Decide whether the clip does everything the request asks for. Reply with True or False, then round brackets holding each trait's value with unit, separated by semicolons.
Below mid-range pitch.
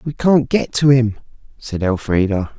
True (120 Hz)